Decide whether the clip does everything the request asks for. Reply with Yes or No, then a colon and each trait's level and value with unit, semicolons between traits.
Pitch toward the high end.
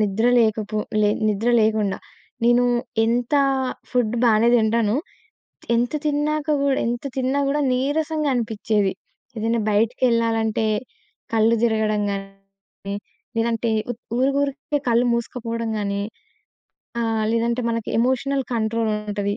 Yes: high, 230 Hz